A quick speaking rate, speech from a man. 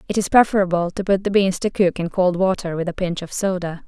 No: fast, 265 wpm; female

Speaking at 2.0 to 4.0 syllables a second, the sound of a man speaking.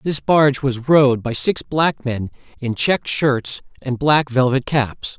Yes: 3.9 syllables/s; male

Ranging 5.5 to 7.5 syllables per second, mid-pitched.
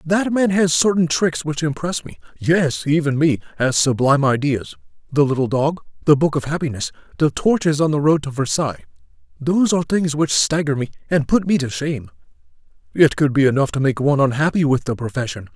Yes: 5.7 syllables/s; medium, 145 Hz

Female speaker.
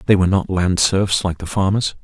No: male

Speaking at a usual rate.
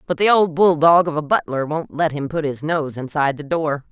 No: fast, 245 wpm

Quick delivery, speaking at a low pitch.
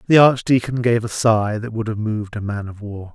Yes: fast, 250 wpm; low, 110 Hz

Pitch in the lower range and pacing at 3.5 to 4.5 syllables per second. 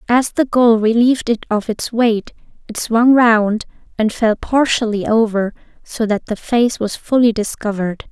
No: high, 225 Hz; 4.4 syllables/s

